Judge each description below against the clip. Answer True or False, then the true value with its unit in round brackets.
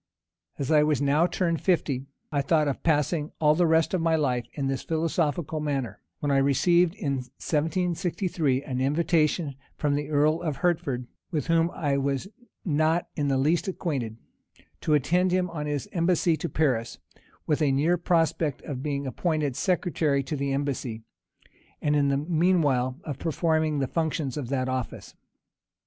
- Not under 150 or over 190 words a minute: True (170 wpm)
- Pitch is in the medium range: True (150 Hz)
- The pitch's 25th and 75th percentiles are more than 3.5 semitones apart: False (3.2 semitones)